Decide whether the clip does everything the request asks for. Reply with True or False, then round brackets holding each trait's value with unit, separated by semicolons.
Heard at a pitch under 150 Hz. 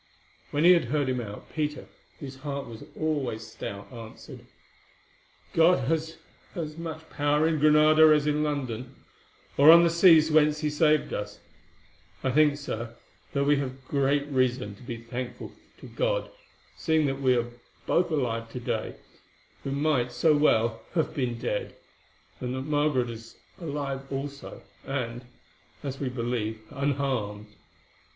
True (140 Hz)